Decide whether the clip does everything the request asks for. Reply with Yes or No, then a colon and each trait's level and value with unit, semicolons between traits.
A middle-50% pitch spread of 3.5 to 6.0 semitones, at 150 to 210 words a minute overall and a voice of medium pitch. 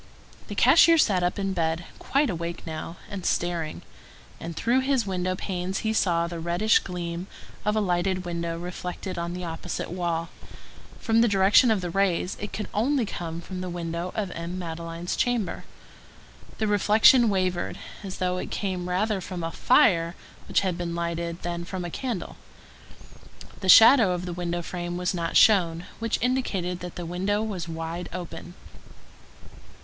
No: average, 3.1 semitones; average, 165 wpm; medium, 180 Hz